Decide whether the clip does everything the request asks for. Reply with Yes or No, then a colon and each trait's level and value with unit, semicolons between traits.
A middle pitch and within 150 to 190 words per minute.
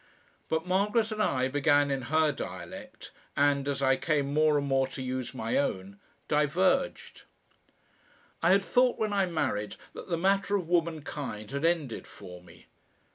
Yes: medium, 150 Hz; average, 160 wpm